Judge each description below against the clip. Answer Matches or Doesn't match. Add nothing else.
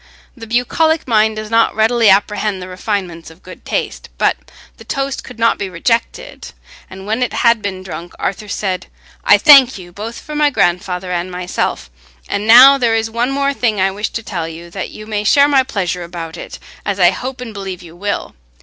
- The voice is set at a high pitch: Matches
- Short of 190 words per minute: Doesn't match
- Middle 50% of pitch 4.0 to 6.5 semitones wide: Matches